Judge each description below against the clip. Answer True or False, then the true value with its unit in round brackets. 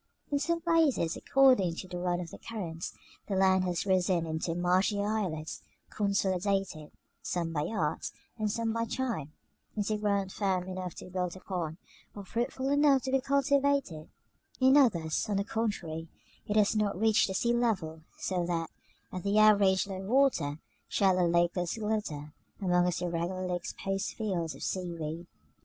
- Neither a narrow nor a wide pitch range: True (4.1 semitones)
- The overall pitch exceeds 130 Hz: True (190 Hz)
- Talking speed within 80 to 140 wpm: False (160 wpm)